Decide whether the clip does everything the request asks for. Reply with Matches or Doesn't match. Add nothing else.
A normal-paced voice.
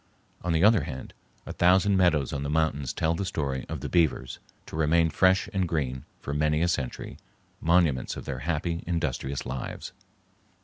Matches